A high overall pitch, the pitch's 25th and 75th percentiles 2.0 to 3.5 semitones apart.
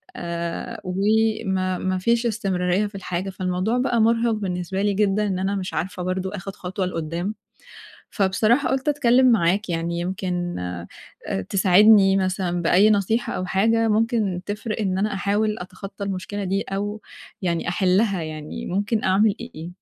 Yes: high, 195 Hz; average, 2.9 semitones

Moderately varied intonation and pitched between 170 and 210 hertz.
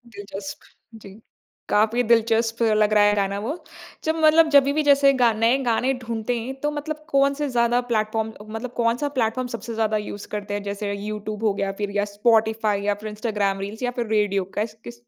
No: average, 3.0 semitones; high, 220 Hz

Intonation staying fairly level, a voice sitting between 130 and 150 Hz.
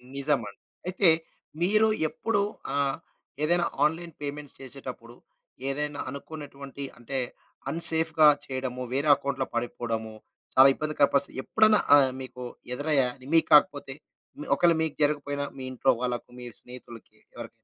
No: average, 3.0 semitones; medium, 140 Hz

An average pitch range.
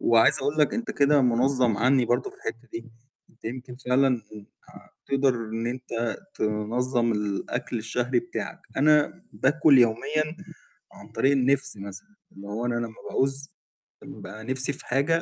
Yes: average, 3.1 semitones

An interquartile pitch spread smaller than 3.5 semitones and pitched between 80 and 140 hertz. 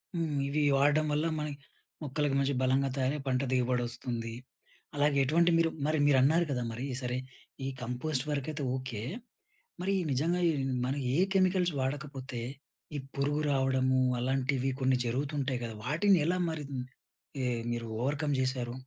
Yes: average, 2.8 semitones; low, 135 Hz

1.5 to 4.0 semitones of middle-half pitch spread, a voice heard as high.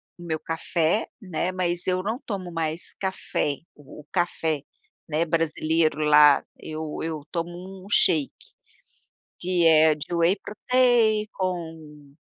No: average, 2.9 semitones; medium, 165 Hz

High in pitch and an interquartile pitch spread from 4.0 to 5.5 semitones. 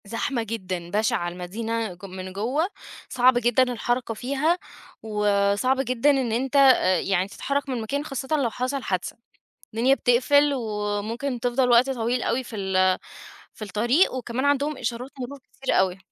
Yes: high, 240 Hz; average, 4.3 semitones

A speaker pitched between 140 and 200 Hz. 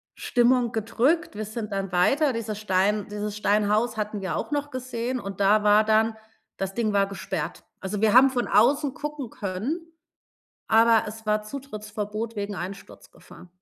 No: high, 215 Hz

